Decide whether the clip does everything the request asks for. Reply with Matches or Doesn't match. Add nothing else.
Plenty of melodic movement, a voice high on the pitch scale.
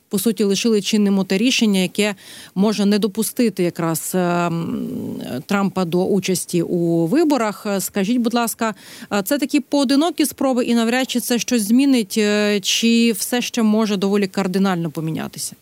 Doesn't match